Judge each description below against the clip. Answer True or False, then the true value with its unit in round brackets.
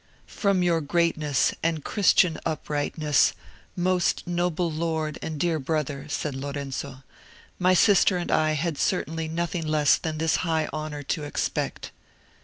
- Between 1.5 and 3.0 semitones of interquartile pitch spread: True (2.5 semitones)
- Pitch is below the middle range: False (160 Hz)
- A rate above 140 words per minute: False (135 wpm)